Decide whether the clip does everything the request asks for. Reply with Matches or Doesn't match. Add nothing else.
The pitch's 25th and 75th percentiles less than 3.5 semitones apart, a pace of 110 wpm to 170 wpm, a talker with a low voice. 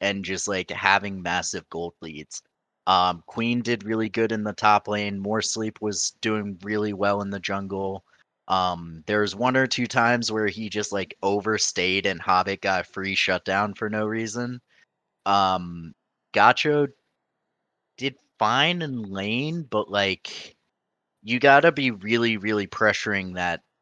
Matches